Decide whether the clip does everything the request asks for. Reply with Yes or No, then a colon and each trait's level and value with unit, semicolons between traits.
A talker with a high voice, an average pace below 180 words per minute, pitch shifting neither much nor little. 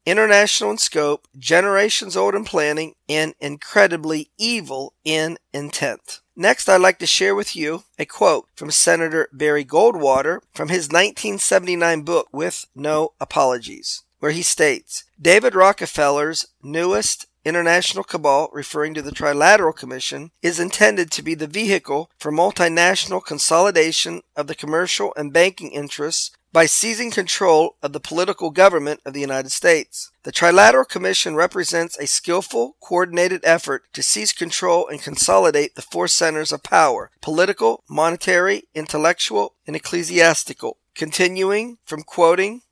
No: medium, 165 Hz; slow, 135 wpm; average, 3.7 semitones